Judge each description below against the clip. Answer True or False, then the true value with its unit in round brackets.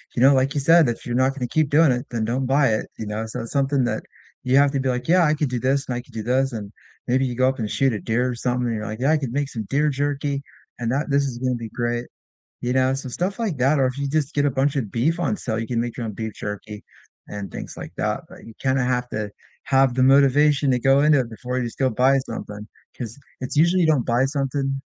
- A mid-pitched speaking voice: False (130 Hz)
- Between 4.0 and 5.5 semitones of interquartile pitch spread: False (2.8 semitones)